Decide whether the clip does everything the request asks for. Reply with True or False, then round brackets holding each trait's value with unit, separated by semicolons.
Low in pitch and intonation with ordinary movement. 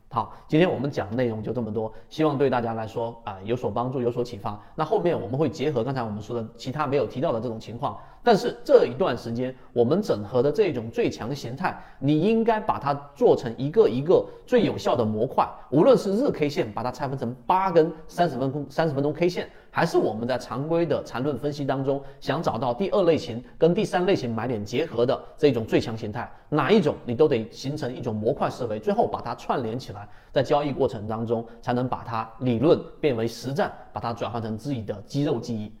True (125 Hz; 4.5 semitones)